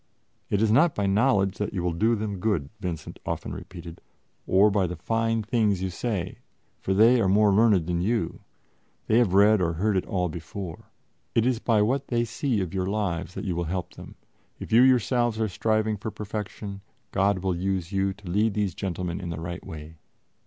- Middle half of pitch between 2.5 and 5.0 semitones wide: Yes, average, 3.5 semitones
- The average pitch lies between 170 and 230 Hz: No, low, 100 Hz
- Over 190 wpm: Yes, average, 200 wpm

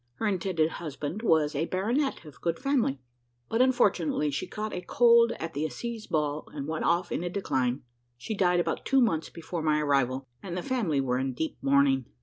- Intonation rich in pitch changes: Yes, wide, 6.7 semitones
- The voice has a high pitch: No, medium, 165 Hz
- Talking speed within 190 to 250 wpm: Yes, average, 195 wpm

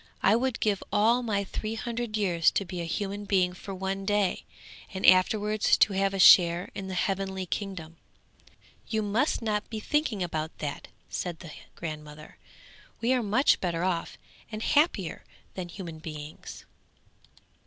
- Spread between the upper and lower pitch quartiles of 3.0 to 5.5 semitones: Yes, average, 3.6 semitones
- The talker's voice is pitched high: Yes, high, 195 Hz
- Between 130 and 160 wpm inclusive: Yes, average, 155 wpm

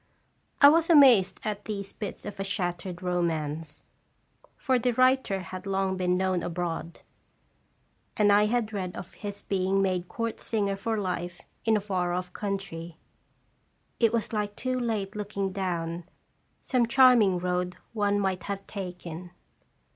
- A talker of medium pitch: No, high, 195 Hz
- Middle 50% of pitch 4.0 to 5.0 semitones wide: No, average, 3.0 semitones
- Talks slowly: No, average, 145 wpm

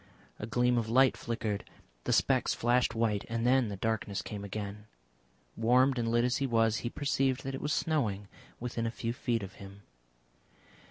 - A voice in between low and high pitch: No, low, 115 Hz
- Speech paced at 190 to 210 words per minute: No, average, 180 wpm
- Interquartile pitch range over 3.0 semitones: No, average, 2.7 semitones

